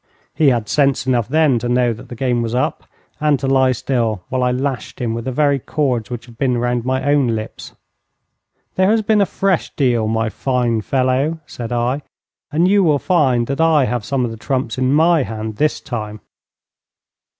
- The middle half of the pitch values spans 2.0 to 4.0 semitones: Yes, average, 3.3 semitones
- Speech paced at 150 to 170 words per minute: No, average, 200 wpm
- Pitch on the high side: No, low, 130 Hz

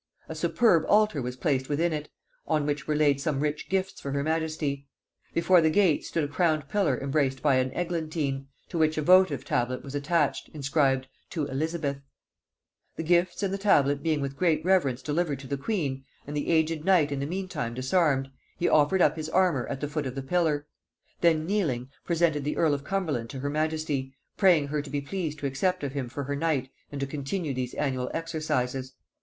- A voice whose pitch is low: No, medium, 150 Hz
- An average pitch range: Yes, average, 3.2 semitones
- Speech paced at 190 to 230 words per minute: Yes, average, 200 wpm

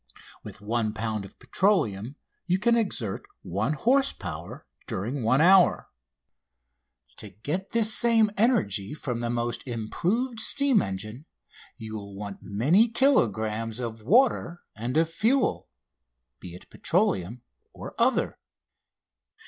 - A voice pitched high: No, low, 120 Hz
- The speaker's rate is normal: No, slow, 125 wpm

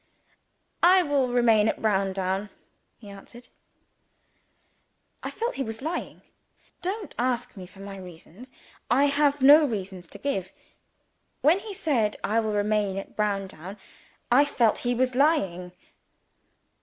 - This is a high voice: Yes, high, 230 Hz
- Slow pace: Yes, slow, 130 wpm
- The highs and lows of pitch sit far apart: Yes, wide, 6.3 semitones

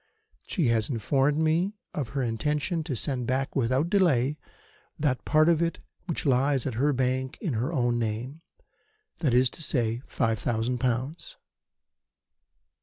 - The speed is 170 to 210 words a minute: No, average, 150 wpm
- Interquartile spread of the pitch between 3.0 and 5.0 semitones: Yes, average, 4.1 semitones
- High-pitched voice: No, low, 130 Hz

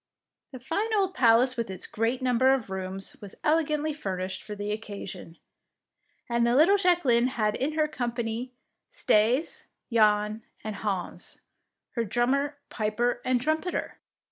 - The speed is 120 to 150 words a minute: Yes, average, 140 wpm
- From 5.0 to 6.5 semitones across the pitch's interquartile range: Yes, average, 5.3 semitones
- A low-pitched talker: No, high, 240 Hz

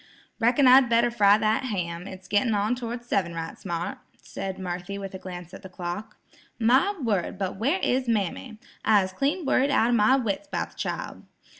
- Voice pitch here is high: Yes, high, 210 Hz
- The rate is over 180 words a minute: Yes, average, 190 wpm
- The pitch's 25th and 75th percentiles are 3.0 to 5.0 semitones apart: Yes, average, 4.5 semitones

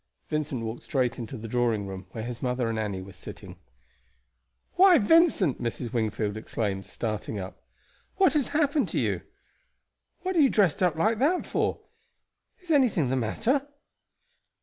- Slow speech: No, average, 155 wpm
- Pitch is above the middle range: No, low, 125 Hz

